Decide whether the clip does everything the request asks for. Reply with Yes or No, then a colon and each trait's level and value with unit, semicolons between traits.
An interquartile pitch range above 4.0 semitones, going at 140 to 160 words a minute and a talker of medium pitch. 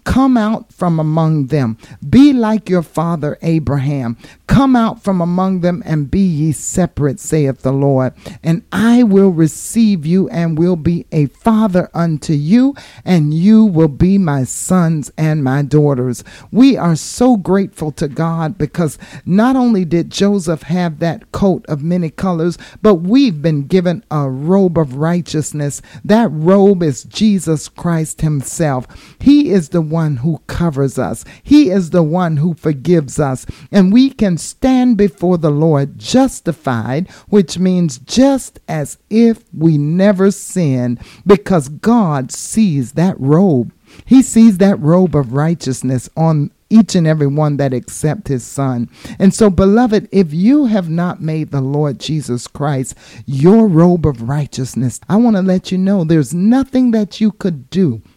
Yes: average, 5.1 semitones; average, 155 wpm; medium, 170 Hz